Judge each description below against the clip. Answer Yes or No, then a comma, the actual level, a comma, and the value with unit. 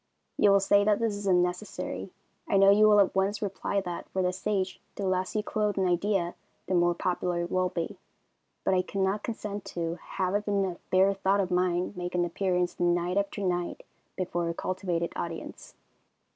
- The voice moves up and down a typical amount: No, narrow, 2.2 semitones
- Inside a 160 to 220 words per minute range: Yes, average, 195 wpm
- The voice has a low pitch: No, medium, 185 Hz